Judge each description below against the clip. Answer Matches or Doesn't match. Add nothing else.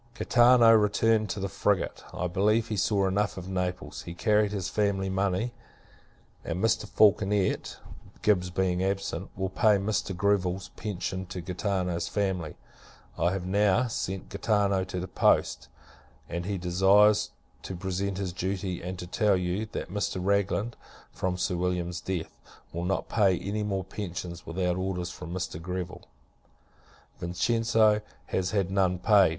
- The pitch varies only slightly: Matches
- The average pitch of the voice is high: Doesn't match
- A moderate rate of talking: Matches